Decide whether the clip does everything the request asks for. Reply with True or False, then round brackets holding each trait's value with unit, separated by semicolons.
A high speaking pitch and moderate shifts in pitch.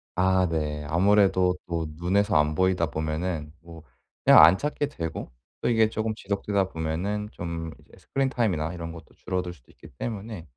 False (90 Hz; 3.8 semitones)